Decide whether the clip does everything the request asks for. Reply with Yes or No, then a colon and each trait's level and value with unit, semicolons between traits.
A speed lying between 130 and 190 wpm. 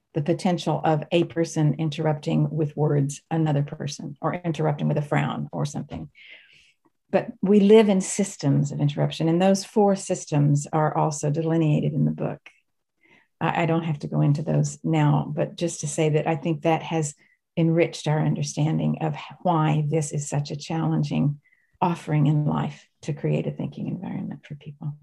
Yes: average, 170 wpm